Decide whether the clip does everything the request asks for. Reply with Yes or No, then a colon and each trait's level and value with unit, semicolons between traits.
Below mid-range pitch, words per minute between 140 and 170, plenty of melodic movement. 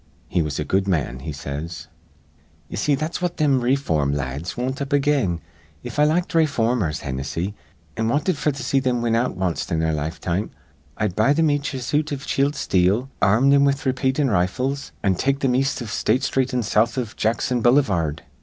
No: low, 120 Hz; average, 200 wpm; wide, 7.6 semitones